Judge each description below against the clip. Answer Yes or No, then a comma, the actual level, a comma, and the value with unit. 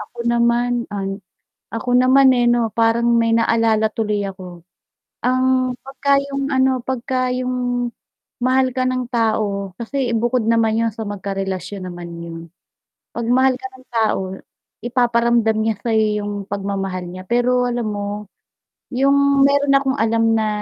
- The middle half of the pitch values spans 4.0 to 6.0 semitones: No, average, 3.1 semitones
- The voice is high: Yes, high, 235 Hz